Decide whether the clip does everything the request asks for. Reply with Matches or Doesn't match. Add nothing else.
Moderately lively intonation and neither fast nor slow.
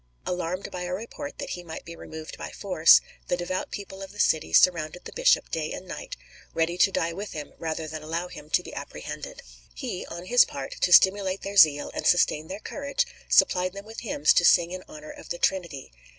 Doesn't match